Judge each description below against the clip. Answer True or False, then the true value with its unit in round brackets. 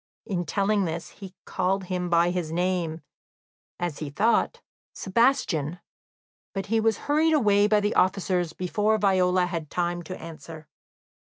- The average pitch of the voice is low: False (185 Hz)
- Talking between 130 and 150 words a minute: True (145 wpm)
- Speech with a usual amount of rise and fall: True (3.1 semitones)